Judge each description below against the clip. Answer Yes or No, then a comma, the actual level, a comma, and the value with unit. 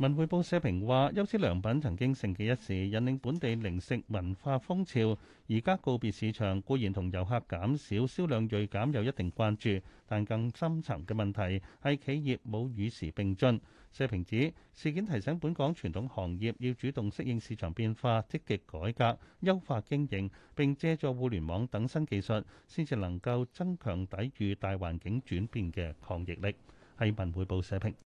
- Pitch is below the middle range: Yes, low, 115 Hz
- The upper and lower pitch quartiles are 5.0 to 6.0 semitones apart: Yes, wide, 5.5 semitones